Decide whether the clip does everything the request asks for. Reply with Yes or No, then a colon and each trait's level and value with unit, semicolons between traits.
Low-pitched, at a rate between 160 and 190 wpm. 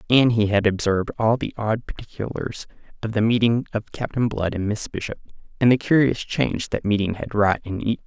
No: low, 110 Hz; average, 200 wpm